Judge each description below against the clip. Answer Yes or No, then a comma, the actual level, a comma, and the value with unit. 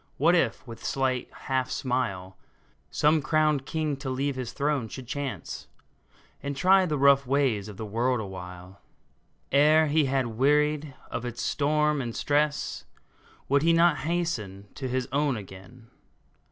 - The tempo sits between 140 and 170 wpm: Yes, average, 150 wpm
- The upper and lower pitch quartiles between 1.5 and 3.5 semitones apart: No, average, 4.1 semitones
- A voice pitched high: No, low, 135 Hz